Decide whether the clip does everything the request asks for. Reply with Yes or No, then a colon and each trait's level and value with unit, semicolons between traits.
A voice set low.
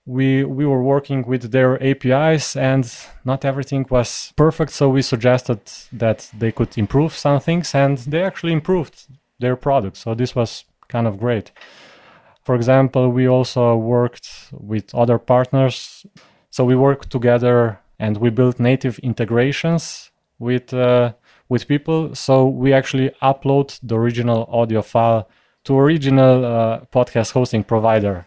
Yes: low, 125 Hz